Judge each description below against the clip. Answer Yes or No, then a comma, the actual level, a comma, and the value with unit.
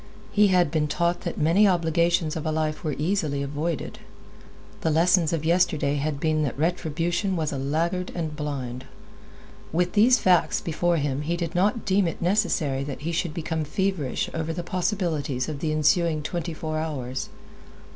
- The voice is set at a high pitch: No, medium, 160 Hz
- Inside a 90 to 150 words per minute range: No, average, 170 wpm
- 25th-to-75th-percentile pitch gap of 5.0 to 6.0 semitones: No, average, 2.8 semitones